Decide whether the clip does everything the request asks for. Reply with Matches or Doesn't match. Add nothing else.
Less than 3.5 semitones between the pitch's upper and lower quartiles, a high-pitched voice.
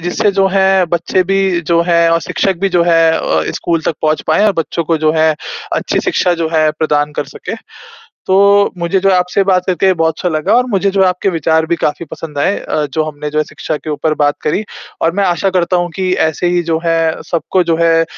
Doesn't match